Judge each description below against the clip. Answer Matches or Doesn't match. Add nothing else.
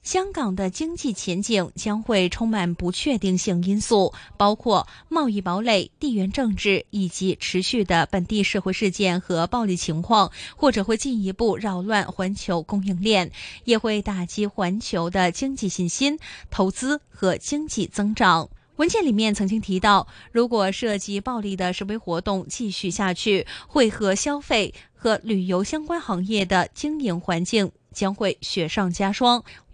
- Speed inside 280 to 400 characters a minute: Doesn't match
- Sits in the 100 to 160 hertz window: Doesn't match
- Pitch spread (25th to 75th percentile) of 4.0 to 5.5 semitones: Doesn't match